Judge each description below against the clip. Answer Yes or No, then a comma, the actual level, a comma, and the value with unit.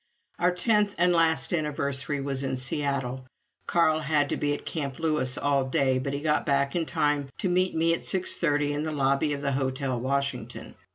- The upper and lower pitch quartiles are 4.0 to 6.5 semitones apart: No, average, 2.8 semitones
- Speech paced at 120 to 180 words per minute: No, average, 195 wpm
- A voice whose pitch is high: No, medium, 145 Hz